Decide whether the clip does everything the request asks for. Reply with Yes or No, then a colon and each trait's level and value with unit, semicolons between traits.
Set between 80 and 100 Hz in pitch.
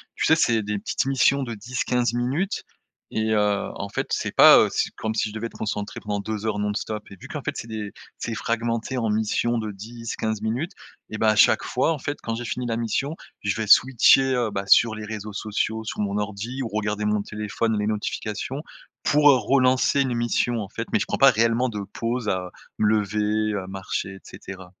No: low, 110 Hz